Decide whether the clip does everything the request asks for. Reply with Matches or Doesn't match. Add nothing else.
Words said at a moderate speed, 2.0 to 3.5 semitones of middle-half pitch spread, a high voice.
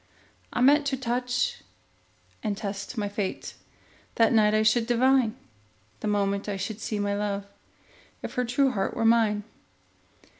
Matches